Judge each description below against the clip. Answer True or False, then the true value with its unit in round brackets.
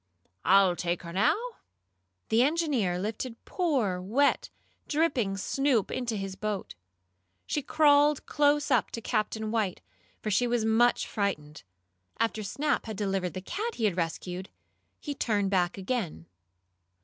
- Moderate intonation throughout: False (5.7 semitones)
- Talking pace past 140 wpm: False (135 wpm)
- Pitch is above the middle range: True (215 Hz)